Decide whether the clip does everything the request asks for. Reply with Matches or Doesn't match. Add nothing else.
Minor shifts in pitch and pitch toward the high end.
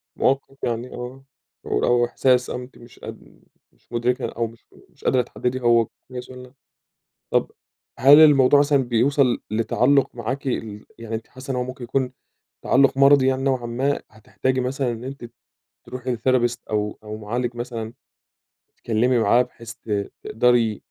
Doesn't match